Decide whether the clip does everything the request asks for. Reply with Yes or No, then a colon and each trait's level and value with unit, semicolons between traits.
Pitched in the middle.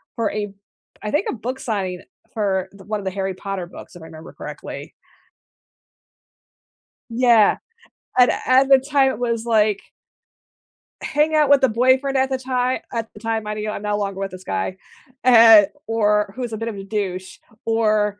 No: high, 215 Hz